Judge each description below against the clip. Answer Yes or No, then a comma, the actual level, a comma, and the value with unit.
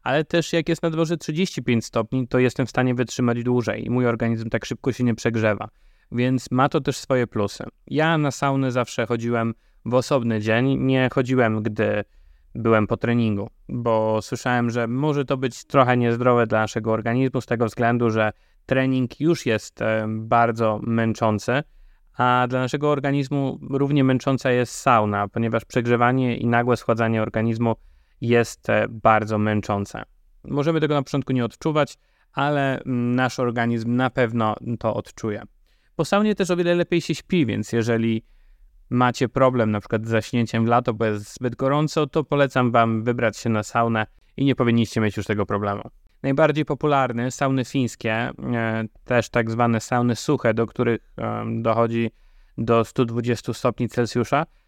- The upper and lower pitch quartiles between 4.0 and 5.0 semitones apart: No, average, 2.7 semitones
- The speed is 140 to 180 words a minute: Yes, fast, 160 wpm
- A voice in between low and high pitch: No, low, 120 Hz